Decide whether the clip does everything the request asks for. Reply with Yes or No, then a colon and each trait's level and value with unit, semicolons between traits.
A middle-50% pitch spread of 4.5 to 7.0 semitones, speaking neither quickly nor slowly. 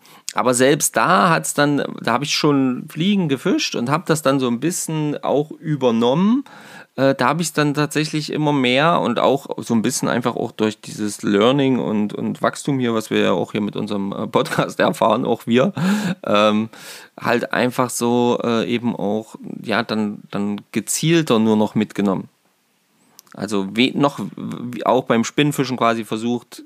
Yes: wide, 5.5 semitones; average, 165 wpm